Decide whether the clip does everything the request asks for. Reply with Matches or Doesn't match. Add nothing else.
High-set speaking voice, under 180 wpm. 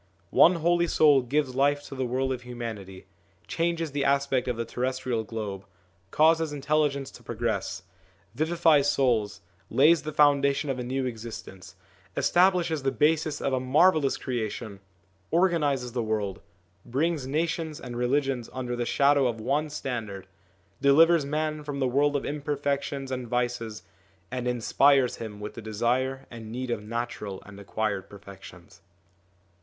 Doesn't match